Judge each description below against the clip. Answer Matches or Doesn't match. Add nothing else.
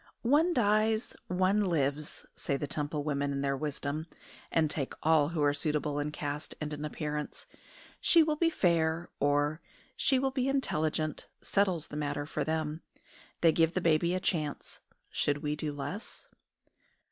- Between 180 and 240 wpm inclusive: Doesn't match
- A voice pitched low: Doesn't match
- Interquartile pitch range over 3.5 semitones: Matches